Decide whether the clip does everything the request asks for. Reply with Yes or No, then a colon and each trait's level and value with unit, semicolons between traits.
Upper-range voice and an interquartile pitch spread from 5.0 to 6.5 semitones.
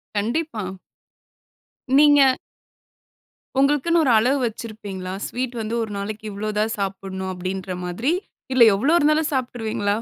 Yes: high, 220 Hz; wide, 5.5 semitones